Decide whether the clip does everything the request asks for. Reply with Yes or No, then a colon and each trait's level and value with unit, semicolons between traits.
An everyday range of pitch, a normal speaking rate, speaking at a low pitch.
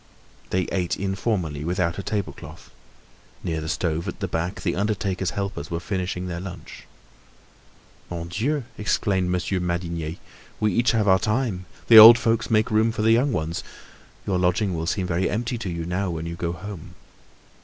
Yes: average, 3.9 semitones; average, 175 wpm; very low, 95 Hz